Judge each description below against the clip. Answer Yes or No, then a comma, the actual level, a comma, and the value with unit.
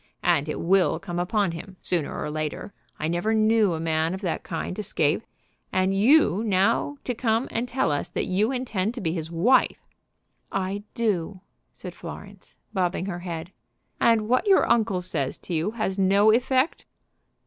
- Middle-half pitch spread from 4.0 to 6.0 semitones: Yes, average, 4.5 semitones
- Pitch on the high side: Yes, high, 195 Hz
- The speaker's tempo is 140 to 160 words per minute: No, average, 170 wpm